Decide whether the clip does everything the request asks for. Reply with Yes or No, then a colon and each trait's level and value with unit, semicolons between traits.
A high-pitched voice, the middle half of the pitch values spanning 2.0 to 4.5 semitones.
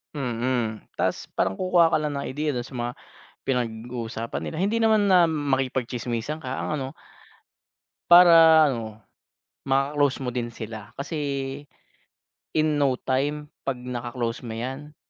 No: low, 135 Hz; average, 3.8 semitones